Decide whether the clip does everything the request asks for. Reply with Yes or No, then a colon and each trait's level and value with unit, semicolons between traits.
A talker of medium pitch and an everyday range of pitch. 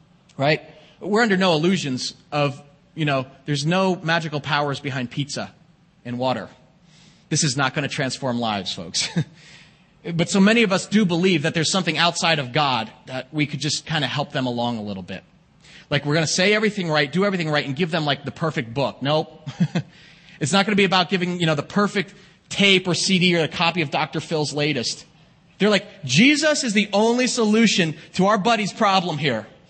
Yes: medium, 165 Hz; average, 4.2 semitones